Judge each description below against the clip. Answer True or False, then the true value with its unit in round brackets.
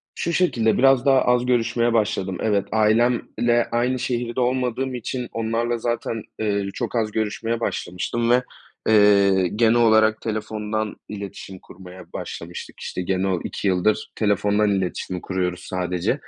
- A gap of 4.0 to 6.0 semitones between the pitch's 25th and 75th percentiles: False (3.2 semitones)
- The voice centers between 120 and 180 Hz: False (110 Hz)